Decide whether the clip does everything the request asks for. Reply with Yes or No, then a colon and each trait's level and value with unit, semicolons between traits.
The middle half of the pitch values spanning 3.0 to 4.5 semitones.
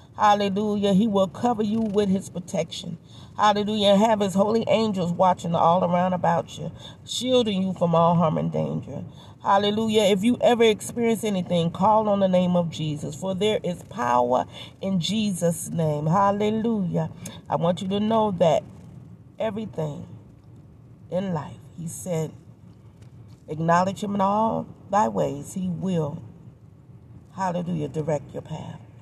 No: average, 5.2 semitones